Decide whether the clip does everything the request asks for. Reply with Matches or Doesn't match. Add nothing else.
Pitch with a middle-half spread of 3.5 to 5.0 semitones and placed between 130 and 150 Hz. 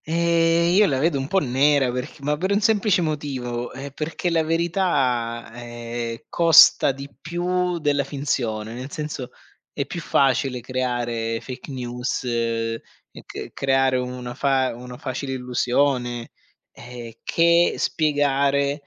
Matches